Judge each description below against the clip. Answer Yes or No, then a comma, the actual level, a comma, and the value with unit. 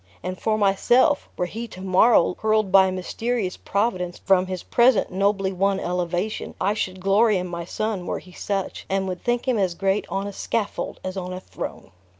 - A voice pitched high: Yes, high, 195 Hz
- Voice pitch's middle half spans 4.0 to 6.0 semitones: No, average, 2.8 semitones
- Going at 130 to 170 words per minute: No, average, 195 wpm